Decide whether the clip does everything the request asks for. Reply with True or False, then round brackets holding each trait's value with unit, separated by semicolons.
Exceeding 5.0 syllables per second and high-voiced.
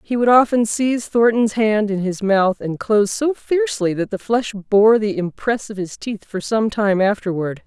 False (4.6 syllables/s; 210 Hz)